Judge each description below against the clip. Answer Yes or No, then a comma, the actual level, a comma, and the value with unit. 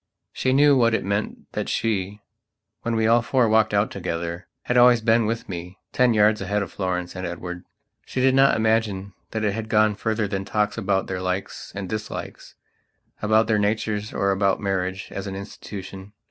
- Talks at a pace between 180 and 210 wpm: Yes, average, 190 wpm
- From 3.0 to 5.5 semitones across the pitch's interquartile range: No, narrow, 2.6 semitones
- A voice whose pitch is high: No, low, 105 Hz